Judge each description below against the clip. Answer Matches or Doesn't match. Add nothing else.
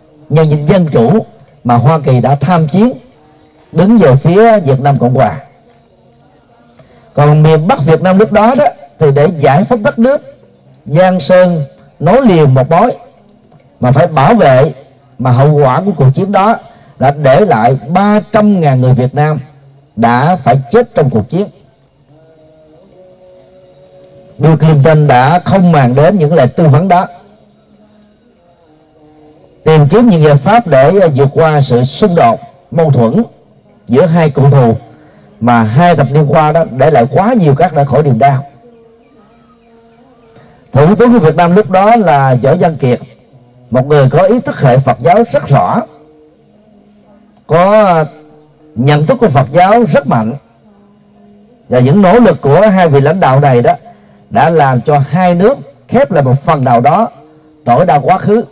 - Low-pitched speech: Doesn't match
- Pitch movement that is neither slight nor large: Doesn't match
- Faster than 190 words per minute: Doesn't match